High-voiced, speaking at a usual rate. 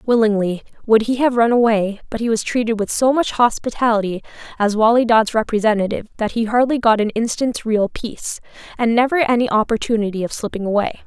Yes: high, 225 Hz; average, 180 wpm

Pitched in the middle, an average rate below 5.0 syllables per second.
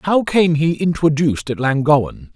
Yes: medium, 150 Hz; 4.8 syllables/s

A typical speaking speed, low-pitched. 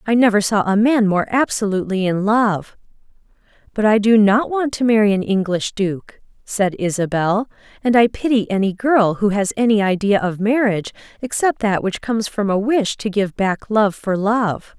No: average, 185 wpm; high, 210 Hz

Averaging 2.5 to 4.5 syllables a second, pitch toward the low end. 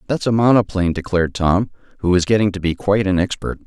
No: 6.8 syllables/s; very low, 95 Hz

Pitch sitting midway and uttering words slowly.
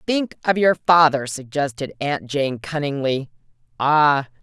Yes: medium, 145 Hz; slow, 110 wpm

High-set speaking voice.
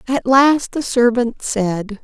Yes: high, 240 Hz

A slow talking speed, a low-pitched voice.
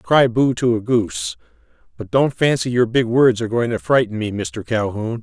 No: fast, 205 wpm; low, 120 Hz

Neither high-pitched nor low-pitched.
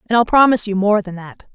No: high, 210 Hz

